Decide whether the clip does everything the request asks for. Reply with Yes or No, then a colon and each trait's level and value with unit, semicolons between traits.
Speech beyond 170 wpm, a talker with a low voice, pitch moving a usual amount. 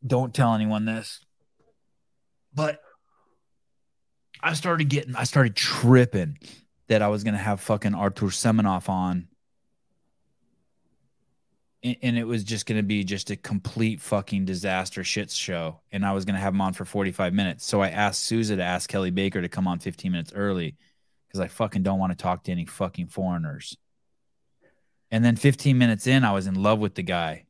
Yes: average, 180 wpm; low, 105 Hz; average, 3.7 semitones